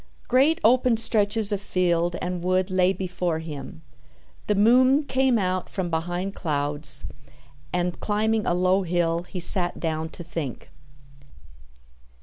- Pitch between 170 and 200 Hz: Yes, medium, 185 Hz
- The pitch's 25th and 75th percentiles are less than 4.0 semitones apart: Yes, average, 3.5 semitones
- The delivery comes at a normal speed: No, slow, 130 wpm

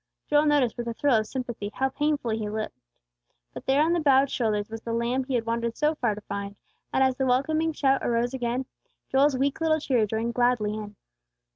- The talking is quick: Yes, fast, 215 wpm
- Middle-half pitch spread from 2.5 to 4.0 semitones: Yes, average, 3.7 semitones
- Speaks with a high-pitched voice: Yes, very high, 250 Hz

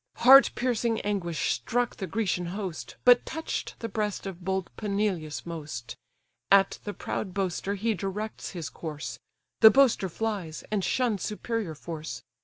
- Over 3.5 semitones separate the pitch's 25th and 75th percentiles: Yes, average, 4.5 semitones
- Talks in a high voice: Yes, high, 200 Hz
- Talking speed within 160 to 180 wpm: No, average, 145 wpm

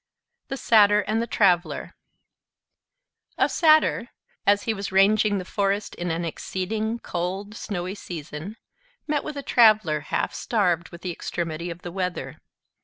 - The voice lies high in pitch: Yes, high, 195 Hz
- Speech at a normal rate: Yes, average, 145 wpm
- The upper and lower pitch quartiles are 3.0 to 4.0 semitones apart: Yes, average, 3.7 semitones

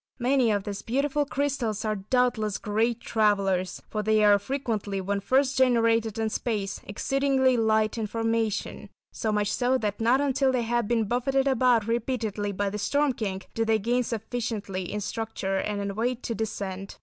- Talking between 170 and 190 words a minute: Yes, average, 175 wpm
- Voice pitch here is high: Yes, high, 225 Hz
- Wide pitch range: No, average, 3.3 semitones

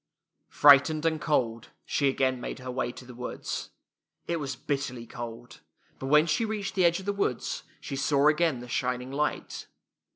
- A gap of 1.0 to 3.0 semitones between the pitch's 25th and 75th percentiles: No, average, 3.8 semitones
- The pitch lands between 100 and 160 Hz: Yes, medium, 140 Hz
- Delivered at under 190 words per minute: Yes, average, 175 wpm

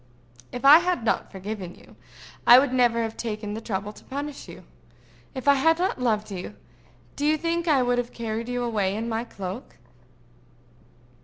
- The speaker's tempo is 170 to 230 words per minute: Yes, average, 180 wpm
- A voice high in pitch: Yes, high, 235 Hz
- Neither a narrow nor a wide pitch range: Yes, average, 4.6 semitones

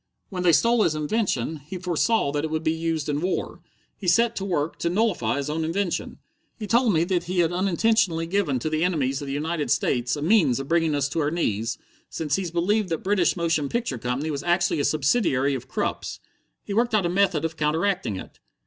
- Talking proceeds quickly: Yes, fast, 220 wpm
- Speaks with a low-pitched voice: No, medium, 165 Hz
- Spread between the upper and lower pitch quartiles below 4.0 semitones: No, average, 4.5 semitones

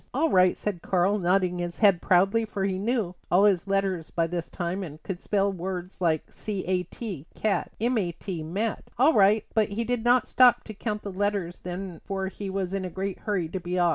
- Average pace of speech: No, fast, 230 wpm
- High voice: Yes, high, 195 Hz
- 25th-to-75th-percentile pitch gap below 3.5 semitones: Yes, average, 2.7 semitones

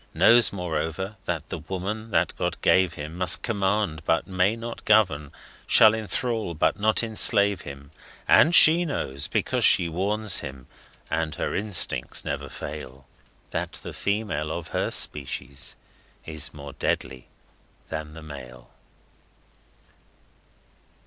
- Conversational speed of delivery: No, slow, 130 wpm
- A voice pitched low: Yes, very low, 90 Hz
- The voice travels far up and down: Yes, wide, 5.8 semitones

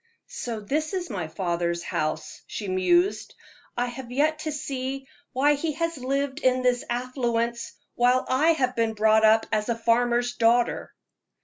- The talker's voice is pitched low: No, high, 245 Hz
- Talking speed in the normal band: Yes, average, 155 wpm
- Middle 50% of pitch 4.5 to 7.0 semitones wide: No, average, 3.6 semitones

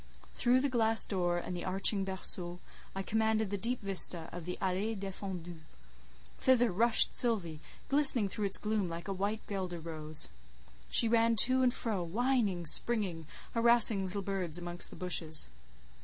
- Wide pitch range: No, average, 4.4 semitones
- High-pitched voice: Yes, high, 195 Hz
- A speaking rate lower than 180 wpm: Yes, average, 155 wpm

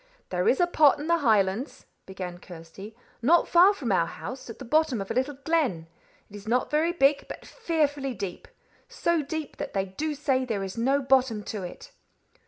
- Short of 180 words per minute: No, average, 195 wpm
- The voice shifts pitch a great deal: Yes, wide, 7.4 semitones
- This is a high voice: Yes, very high, 260 Hz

